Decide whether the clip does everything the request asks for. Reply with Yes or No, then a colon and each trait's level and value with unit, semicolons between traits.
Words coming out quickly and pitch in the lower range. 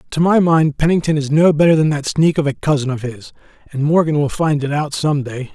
No: fast, 250 wpm; medium, 150 Hz